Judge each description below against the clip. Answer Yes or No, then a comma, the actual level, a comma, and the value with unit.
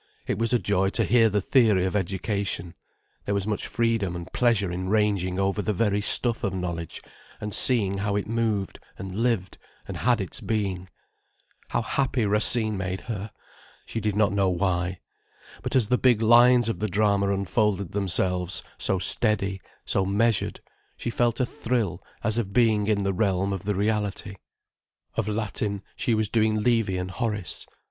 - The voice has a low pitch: Yes, low, 105 Hz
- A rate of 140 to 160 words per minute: No, average, 170 wpm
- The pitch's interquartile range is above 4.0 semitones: No, average, 2.8 semitones